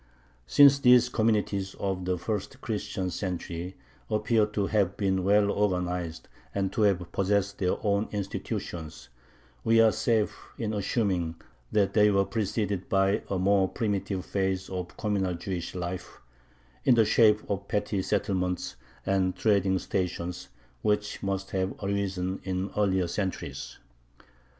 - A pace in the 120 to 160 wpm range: Yes, slow, 135 wpm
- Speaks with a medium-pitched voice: No, low, 100 Hz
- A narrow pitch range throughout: Yes, narrow, 2.1 semitones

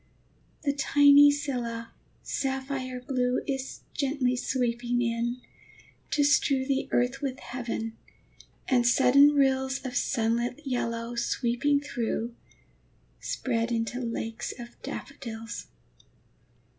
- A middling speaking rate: No, slow, 100 wpm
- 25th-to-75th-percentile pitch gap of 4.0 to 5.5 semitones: No, narrow, 2.6 semitones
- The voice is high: Yes, very high, 250 Hz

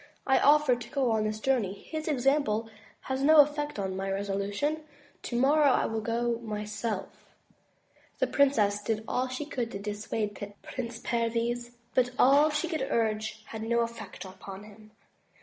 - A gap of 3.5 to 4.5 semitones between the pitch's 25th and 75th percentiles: Yes, average, 4.2 semitones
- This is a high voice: Yes, high, 230 Hz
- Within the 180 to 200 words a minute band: No, average, 160 wpm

